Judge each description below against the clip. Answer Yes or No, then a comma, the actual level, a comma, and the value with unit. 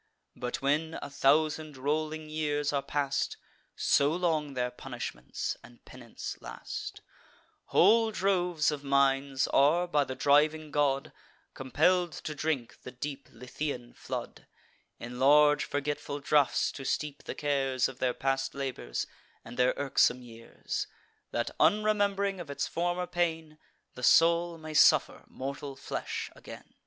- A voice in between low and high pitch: Yes, medium, 145 Hz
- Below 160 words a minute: Yes, slow, 135 wpm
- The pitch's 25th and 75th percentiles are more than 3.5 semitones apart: No, average, 2.9 semitones